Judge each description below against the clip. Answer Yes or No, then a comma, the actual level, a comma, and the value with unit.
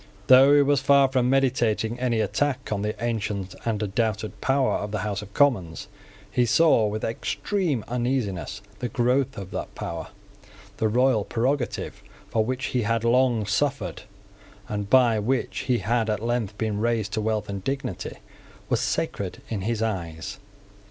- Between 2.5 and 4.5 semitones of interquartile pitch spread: Yes, average, 3.5 semitones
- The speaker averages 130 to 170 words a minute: Yes, average, 160 wpm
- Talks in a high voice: No, low, 115 Hz